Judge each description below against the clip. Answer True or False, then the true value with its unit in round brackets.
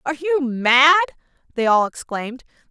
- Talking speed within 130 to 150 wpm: True (135 wpm)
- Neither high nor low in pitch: False (275 Hz)